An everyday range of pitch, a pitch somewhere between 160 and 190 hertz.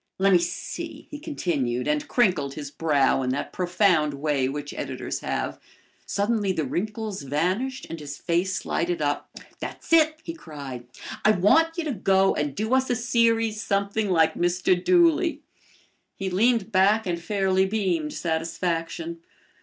No: wide, 5.9 semitones; medium, 185 Hz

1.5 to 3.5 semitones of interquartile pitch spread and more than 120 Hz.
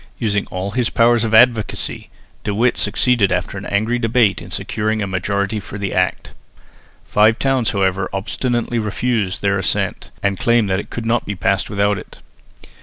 No: average, 3.0 semitones; low, 105 Hz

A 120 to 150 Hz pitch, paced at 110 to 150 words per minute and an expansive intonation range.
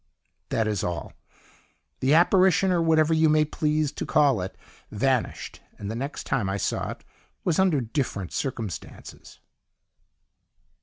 Yes: medium, 140 Hz; average, 140 wpm; wide, 6.4 semitones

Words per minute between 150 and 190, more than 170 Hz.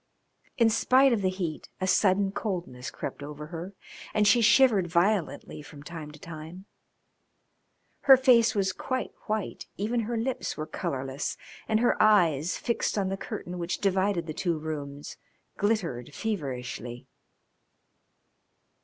No: slow, 135 wpm; medium, 185 Hz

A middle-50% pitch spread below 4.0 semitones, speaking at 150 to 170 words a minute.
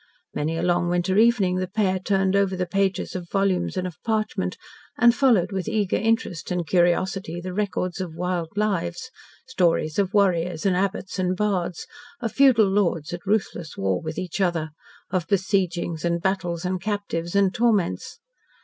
Yes: narrow, 2.5 semitones; average, 165 wpm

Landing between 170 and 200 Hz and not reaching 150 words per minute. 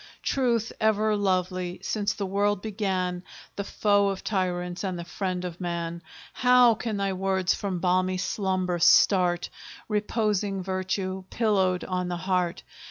Yes: high, 190 Hz; average, 140 wpm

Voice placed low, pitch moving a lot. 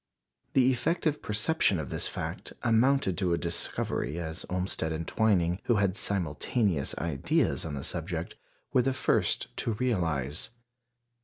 Yes: very low, 90 Hz; wide, 6.1 semitones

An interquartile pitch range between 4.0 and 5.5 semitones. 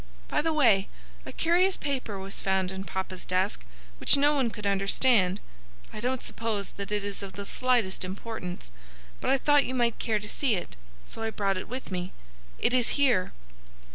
Yes: average, 4.9 semitones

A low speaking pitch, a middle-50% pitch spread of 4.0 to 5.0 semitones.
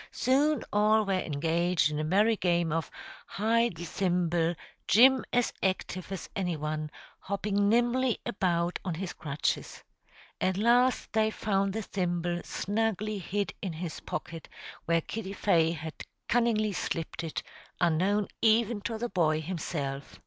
No: high, 190 Hz; average, 4.5 semitones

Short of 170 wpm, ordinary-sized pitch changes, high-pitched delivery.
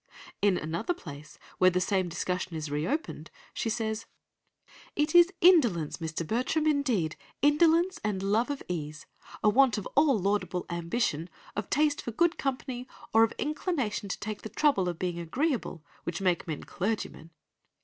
No: average, 150 wpm; wide, 8.4 semitones; high, 210 Hz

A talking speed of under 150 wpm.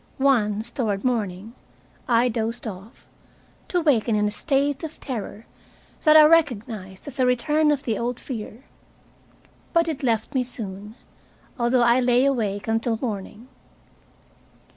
Yes: average, 140 wpm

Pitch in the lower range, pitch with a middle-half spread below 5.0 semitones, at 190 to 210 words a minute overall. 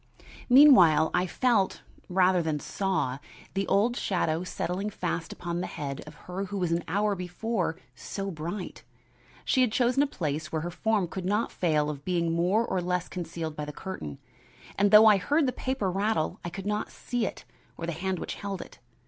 No: medium, 180 Hz; average, 3.9 semitones; average, 195 wpm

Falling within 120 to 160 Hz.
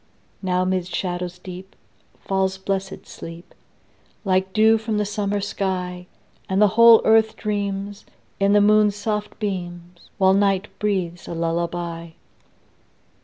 No: high, 190 Hz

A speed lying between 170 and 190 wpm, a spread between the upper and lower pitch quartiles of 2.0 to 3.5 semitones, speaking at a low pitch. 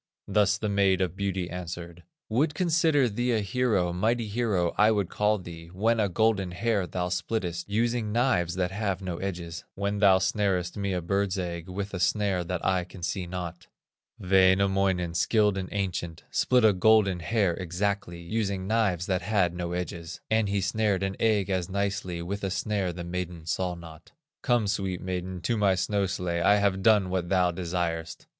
Yes: average, 180 wpm; average, 2.8 semitones; very low, 95 Hz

